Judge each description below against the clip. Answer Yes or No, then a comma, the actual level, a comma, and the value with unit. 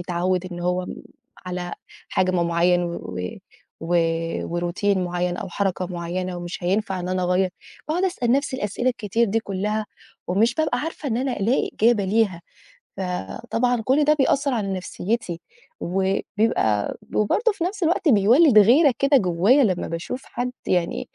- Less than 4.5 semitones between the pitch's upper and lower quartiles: No, wide, 5.6 semitones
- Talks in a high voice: Yes, high, 200 Hz